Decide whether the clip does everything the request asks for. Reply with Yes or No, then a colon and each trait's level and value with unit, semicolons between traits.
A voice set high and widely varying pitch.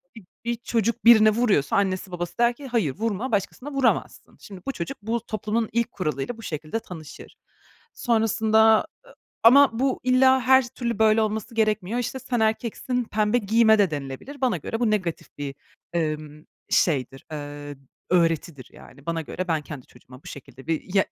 Yes: high, 215 Hz; wide, 6.3 semitones